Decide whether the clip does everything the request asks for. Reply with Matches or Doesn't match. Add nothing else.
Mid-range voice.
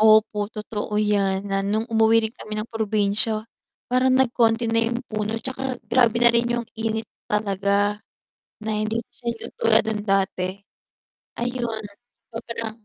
Doesn't match